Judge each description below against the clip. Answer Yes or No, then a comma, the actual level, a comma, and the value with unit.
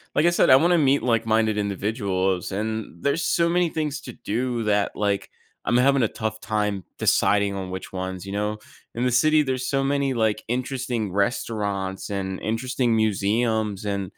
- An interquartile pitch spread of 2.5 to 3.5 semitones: No, average, 4.2 semitones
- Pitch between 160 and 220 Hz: No, low, 110 Hz